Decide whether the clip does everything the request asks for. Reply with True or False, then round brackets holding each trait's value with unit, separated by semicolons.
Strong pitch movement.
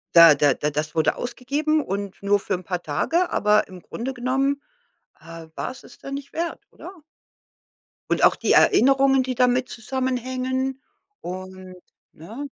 True (6.5 semitones)